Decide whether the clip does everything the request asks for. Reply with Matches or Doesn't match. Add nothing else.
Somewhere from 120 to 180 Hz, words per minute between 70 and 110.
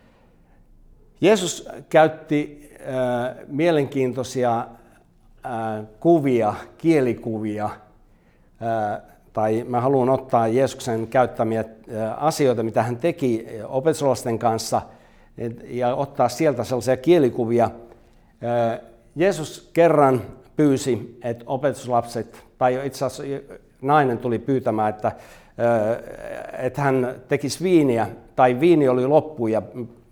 Matches